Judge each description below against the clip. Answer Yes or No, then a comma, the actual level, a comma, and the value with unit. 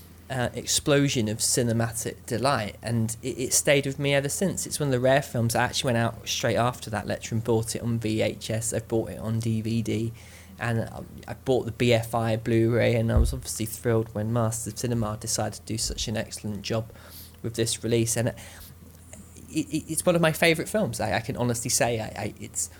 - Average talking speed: No, fast, 210 wpm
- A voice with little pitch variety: Yes, narrow, 2.3 semitones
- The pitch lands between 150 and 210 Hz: No, low, 115 Hz